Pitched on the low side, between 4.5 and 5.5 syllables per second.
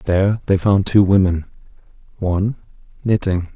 Yes: very low, 95 Hz; 4.9 syllables/s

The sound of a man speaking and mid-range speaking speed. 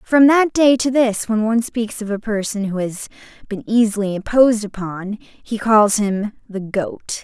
No: female; average, 185 wpm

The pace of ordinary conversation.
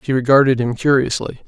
Yes: average, 165 wpm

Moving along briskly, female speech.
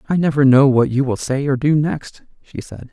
No: fast, 245 wpm; male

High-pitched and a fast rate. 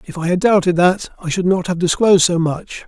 No: medium, 180 Hz; fast, 250 wpm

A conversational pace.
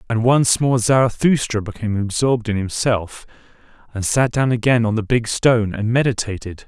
Yes: average, 160 wpm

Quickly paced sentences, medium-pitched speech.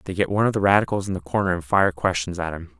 No: fast, 300 wpm; very low, 90 Hz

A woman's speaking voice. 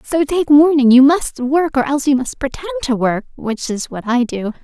Yes: female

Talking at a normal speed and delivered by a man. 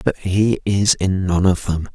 No: fast, 215 wpm; male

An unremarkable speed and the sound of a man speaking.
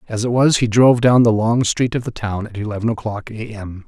No: fast, 265 wpm; male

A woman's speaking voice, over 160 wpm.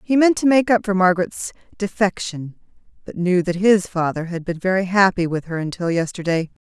Yes: female; average, 190 wpm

